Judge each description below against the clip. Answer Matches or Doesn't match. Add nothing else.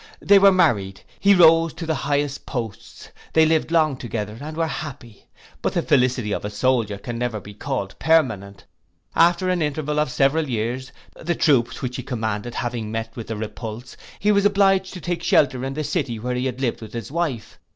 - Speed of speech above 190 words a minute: Matches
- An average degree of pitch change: Doesn't match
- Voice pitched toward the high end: Doesn't match